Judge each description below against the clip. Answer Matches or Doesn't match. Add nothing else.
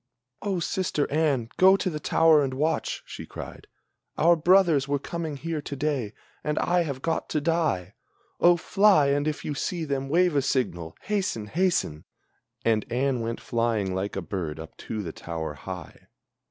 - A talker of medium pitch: Matches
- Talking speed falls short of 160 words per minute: Doesn't match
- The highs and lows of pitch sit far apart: Matches